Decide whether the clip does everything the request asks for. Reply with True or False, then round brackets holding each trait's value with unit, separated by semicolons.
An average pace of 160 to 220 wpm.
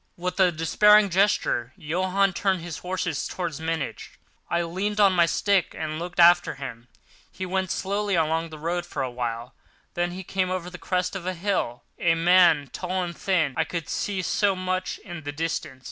True (190 wpm)